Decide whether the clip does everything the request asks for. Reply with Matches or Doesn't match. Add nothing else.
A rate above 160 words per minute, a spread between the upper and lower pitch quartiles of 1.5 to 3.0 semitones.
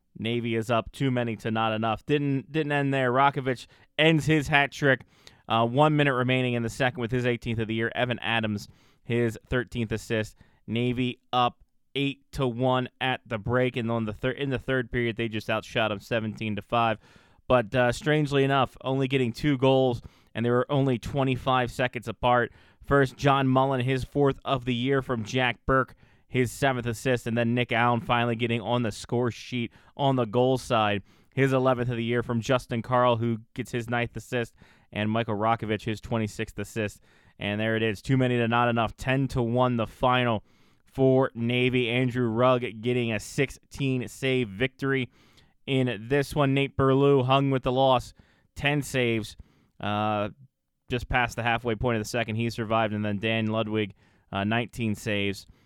Matches